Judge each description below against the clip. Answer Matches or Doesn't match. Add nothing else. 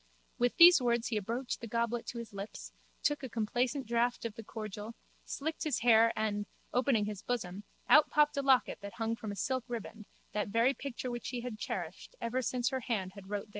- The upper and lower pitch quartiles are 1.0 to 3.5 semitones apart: Matches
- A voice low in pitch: Doesn't match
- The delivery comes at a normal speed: Doesn't match